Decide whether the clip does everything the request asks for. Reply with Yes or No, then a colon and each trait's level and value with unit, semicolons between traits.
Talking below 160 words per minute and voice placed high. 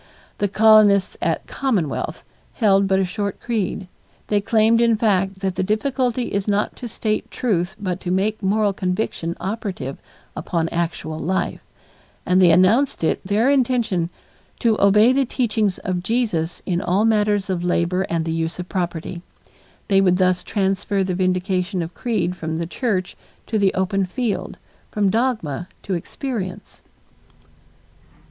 Yes: average, 150 wpm; high, 195 Hz